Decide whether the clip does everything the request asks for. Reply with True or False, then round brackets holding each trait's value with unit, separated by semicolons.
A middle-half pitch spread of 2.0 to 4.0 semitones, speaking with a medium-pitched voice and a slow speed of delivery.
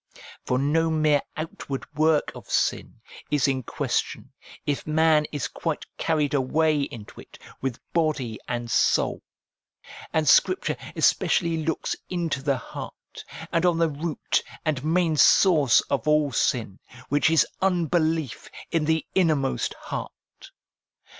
True (2.7 semitones; 155 Hz; 130 wpm)